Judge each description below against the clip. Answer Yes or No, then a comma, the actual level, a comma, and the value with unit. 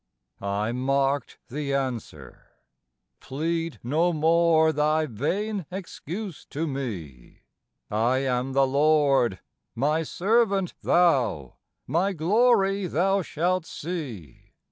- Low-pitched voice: No, medium, 150 Hz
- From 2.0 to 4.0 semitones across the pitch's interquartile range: No, average, 5.1 semitones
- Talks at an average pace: No, slow, 100 wpm